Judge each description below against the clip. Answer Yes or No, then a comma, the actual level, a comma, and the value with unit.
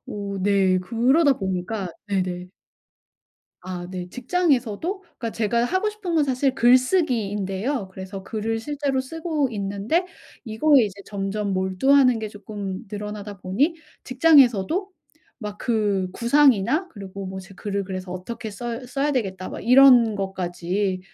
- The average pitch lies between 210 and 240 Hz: Yes, high, 215 Hz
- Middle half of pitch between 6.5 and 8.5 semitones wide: No, wide, 5.4 semitones